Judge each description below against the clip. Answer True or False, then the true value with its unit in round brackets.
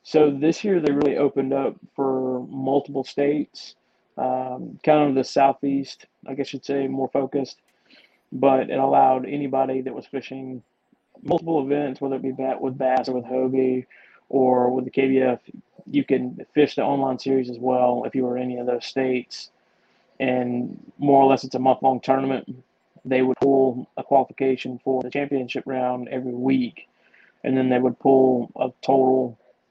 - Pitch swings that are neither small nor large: False (1.2 semitones)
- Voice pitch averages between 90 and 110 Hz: False (130 Hz)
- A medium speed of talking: True (170 wpm)